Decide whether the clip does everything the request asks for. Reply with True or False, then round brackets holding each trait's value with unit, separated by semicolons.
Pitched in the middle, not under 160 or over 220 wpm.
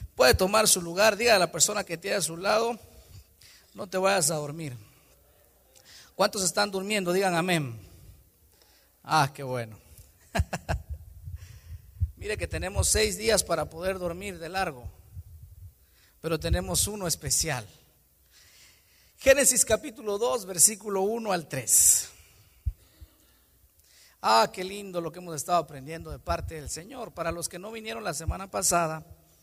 False (165 Hz; 135 wpm)